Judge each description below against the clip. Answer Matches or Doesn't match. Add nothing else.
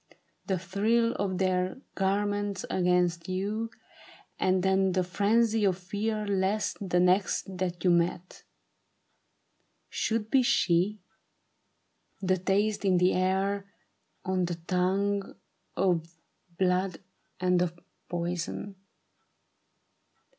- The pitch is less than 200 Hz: Matches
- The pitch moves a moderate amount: Doesn't match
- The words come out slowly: Matches